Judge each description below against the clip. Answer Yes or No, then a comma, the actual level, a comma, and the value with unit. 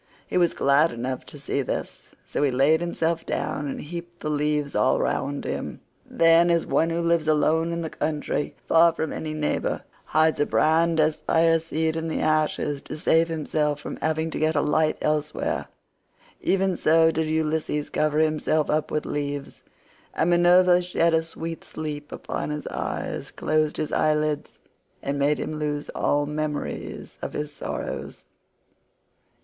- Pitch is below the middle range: No, medium, 155 Hz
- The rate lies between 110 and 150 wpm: No, average, 165 wpm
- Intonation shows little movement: Yes, narrow, 1.7 semitones